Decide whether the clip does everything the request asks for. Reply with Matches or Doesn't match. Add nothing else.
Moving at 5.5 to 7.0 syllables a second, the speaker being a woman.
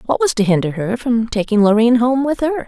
Matches